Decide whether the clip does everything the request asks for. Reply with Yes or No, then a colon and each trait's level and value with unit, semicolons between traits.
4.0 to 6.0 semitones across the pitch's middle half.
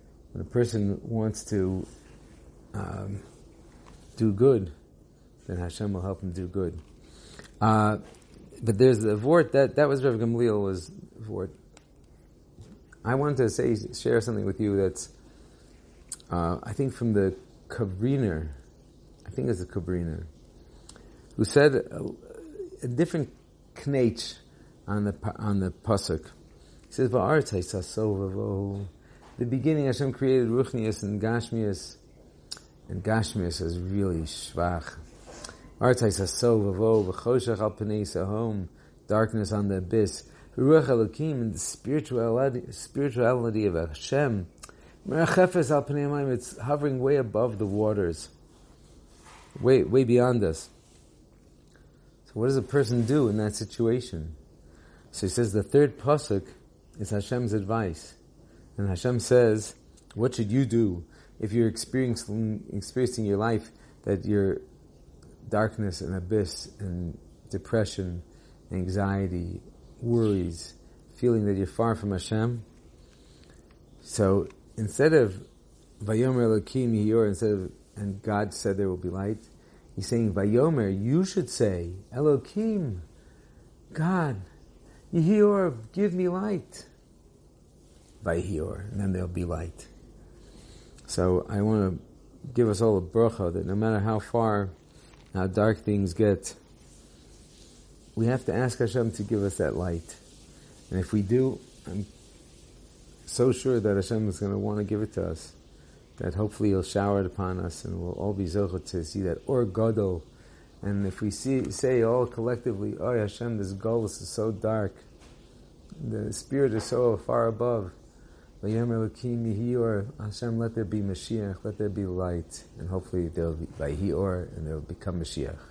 Yes: average, 4.4 semitones